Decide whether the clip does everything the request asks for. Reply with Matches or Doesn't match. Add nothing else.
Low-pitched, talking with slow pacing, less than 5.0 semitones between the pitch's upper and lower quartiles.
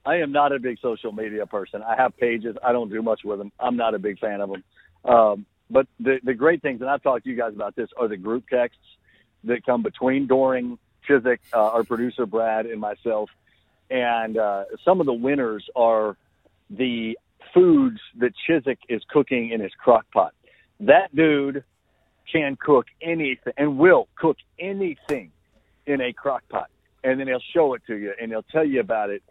Doesn't match